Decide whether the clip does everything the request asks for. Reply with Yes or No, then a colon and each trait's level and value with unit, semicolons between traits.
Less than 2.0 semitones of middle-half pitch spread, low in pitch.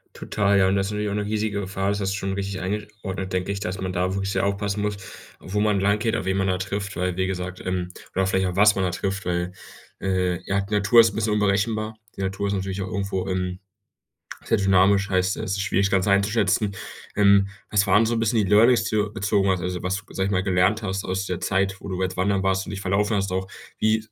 Yes: narrow, 1.5 semitones; low, 100 Hz